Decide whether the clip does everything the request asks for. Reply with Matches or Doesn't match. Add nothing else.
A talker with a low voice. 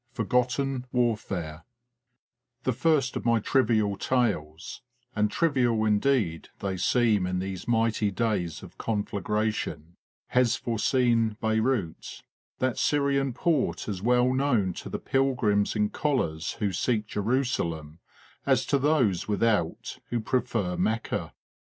Matches